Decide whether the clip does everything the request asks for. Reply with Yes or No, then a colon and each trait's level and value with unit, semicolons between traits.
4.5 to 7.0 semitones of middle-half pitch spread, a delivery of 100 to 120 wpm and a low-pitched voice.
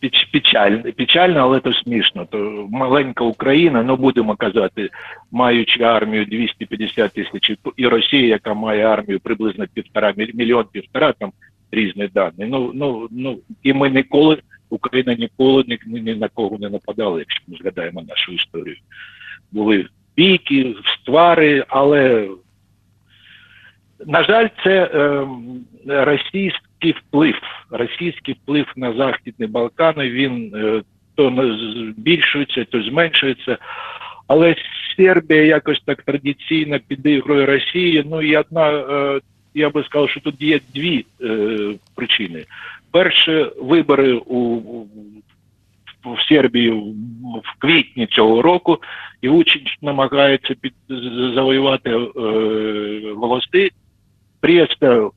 Yes: average, 4.8 semitones; average, 115 wpm; low, 130 Hz